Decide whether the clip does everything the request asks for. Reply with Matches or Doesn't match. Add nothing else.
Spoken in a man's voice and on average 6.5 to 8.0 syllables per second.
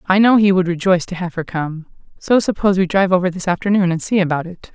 Doesn't match